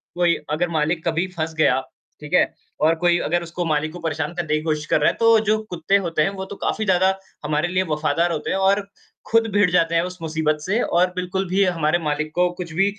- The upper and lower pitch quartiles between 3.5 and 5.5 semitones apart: No, average, 3.0 semitones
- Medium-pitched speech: Yes, medium, 170 Hz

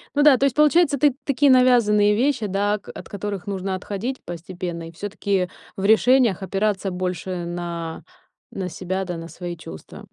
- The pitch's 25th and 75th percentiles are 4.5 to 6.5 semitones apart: Yes, average, 5.3 semitones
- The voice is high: Yes, high, 195 Hz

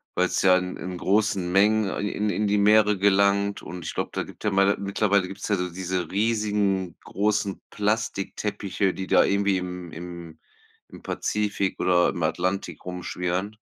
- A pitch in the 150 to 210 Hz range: No, low, 100 Hz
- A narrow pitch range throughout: Yes, narrow, 2.1 semitones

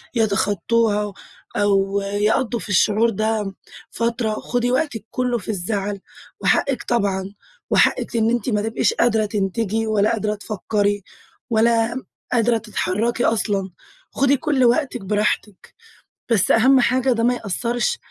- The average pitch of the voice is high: Yes, high, 220 Hz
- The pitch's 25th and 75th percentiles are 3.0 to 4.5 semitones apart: No, narrow, 2.6 semitones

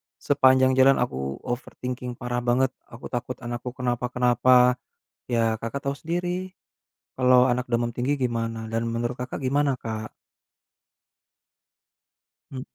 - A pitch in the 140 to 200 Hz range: No, low, 125 Hz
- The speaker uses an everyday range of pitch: No, narrow, 1.7 semitones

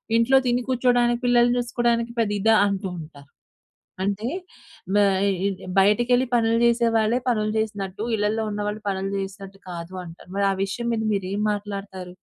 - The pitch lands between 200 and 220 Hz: Yes, high, 210 Hz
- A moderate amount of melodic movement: Yes, average, 3.3 semitones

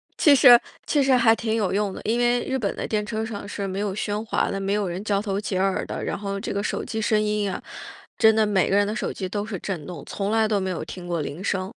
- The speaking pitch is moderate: No, high, 205 Hz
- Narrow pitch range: Yes, narrow, 2.1 semitones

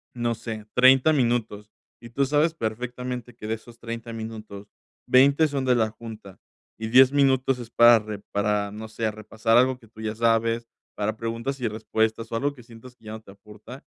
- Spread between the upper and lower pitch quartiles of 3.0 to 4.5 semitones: No, narrow, 2.4 semitones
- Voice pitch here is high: No, low, 115 Hz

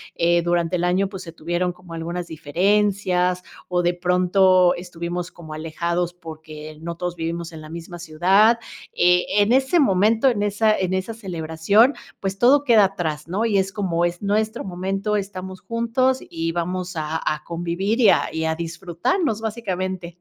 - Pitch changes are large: No, average, 3.1 semitones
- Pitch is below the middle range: No, medium, 180 Hz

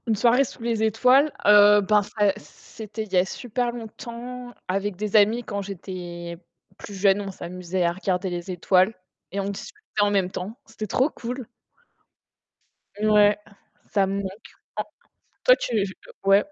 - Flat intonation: No, average, 3.0 semitones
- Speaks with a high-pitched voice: Yes, high, 205 Hz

